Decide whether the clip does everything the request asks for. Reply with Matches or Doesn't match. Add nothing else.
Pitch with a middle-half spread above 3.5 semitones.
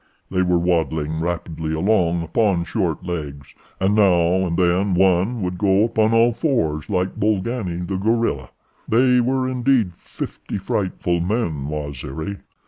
Matches